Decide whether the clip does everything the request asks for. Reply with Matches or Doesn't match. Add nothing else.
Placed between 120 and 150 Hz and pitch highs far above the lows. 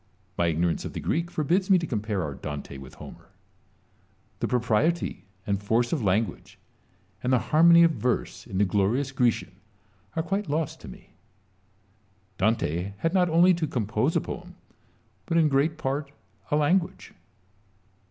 Matches